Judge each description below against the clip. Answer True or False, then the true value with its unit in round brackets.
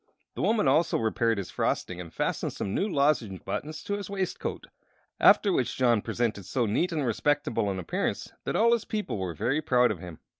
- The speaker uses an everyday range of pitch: False (8.0 semitones)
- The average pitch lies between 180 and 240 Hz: False (125 Hz)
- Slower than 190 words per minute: False (195 wpm)